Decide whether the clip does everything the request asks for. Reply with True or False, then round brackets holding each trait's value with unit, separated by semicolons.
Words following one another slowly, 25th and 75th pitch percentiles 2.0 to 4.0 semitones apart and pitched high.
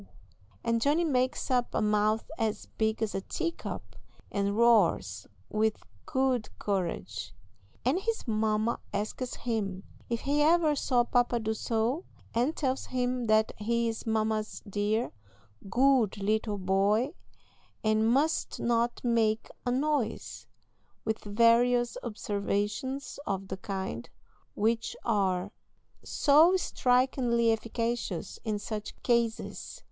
True (120 wpm; 3.0 semitones; 225 Hz)